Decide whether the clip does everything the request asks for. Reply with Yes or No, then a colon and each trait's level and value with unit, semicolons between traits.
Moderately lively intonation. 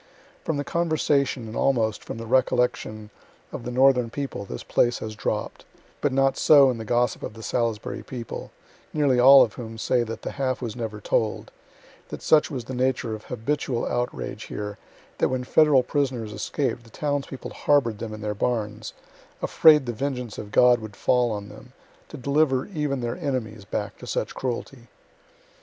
Yes: average, 3.5 semitones